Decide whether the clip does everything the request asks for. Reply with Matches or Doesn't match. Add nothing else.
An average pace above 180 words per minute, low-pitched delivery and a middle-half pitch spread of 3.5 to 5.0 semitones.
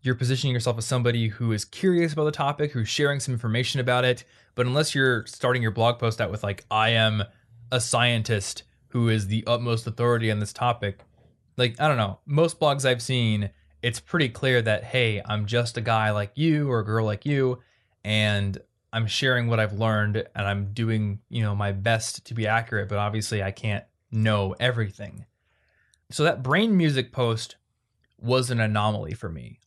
Doesn't match